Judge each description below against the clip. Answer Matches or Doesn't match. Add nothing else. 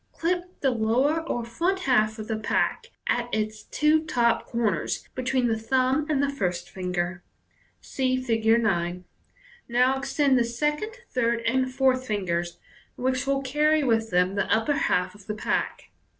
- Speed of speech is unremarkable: Matches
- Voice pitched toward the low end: Doesn't match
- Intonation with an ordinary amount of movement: Matches